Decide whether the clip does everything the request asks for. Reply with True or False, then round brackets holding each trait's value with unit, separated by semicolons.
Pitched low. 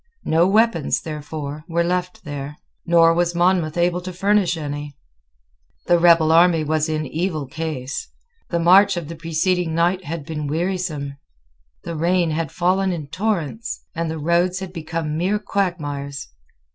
False (165 Hz)